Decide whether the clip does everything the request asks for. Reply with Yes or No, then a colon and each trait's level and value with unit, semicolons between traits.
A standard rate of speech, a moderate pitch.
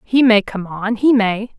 No: average, 190 wpm; high, 220 Hz